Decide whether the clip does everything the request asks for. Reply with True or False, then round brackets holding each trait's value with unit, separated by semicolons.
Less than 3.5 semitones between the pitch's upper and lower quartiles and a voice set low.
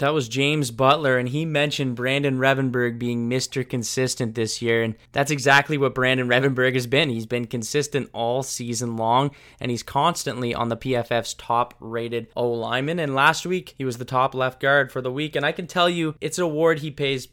True (2.8 semitones; 130 Hz)